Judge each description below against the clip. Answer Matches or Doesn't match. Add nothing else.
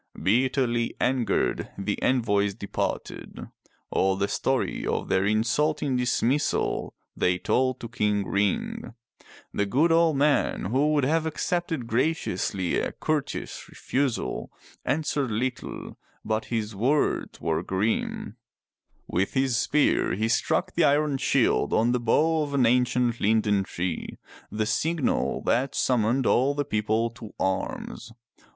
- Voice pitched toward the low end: Matches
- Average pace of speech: Doesn't match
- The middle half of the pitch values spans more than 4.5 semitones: Matches